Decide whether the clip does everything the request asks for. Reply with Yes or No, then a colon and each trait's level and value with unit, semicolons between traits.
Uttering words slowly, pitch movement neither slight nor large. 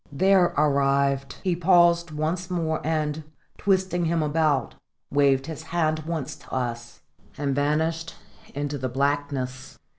Yes: slow, 125 wpm; average, 3.3 semitones